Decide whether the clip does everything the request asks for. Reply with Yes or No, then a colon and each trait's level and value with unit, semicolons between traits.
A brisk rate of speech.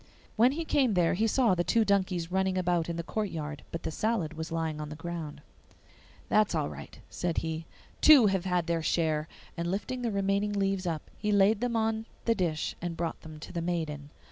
Yes: fast, 210 wpm